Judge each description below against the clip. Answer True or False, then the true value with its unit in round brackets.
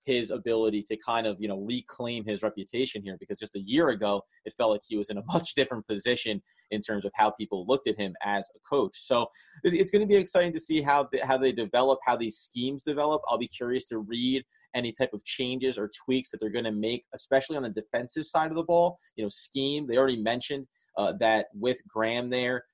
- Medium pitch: False (120 Hz)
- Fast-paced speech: True (235 wpm)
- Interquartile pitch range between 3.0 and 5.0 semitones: True (3.8 semitones)